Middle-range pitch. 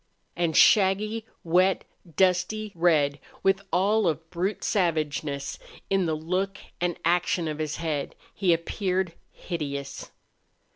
Yes: medium, 175 Hz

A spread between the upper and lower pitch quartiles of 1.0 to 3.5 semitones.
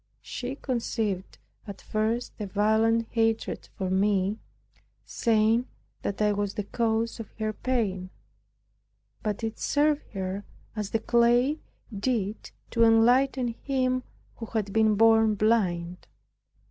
Yes: narrow, 2.5 semitones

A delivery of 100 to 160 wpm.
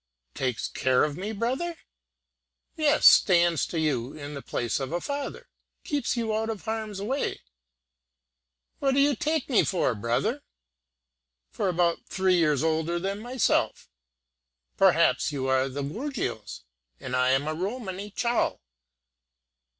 Yes: average, 145 wpm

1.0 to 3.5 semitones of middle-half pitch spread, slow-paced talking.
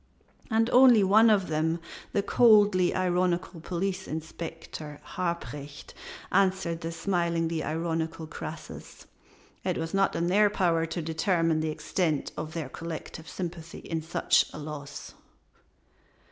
Yes: average, 2.7 semitones; slow, 125 wpm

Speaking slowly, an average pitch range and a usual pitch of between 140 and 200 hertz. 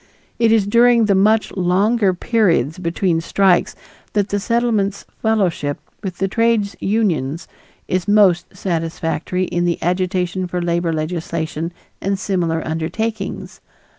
Yes: slow, 120 wpm; average, 3.5 semitones; medium, 185 Hz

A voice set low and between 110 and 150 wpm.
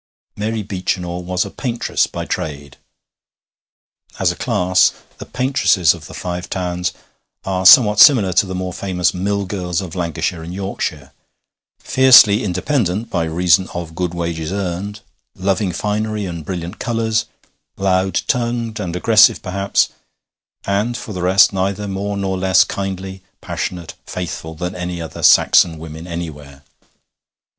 Yes: very low, 95 Hz; average, 140 wpm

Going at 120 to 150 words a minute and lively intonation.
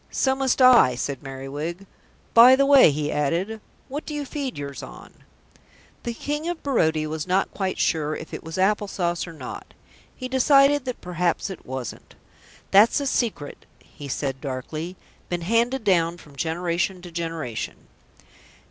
No: average, 160 wpm; wide, 8.3 semitones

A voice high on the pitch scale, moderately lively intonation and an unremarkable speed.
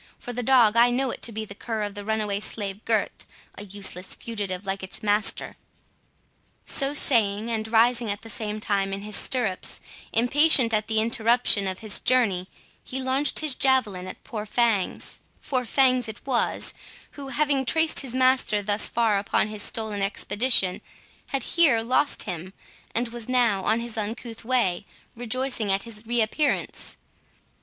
Yes: high, 225 Hz; average, 3.5 semitones; average, 165 wpm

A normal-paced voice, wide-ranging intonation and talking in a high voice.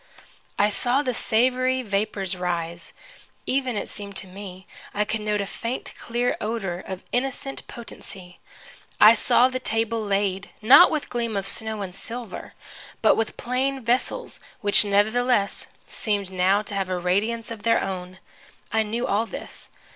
No: average, 155 wpm; average, 3.6 semitones; high, 215 Hz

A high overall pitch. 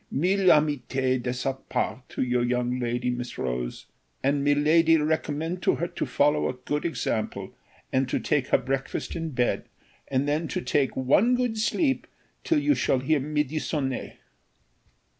No: medium, 140 Hz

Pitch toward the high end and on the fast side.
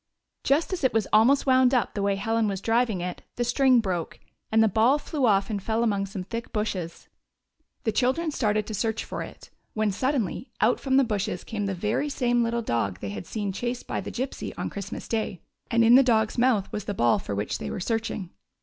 Yes: high, 220 Hz; fast, 220 wpm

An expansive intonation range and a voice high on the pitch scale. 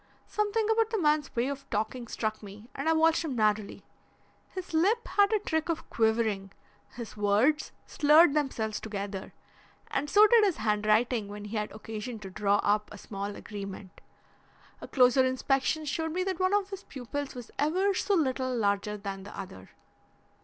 Yes: wide, 7.4 semitones; very high, 250 Hz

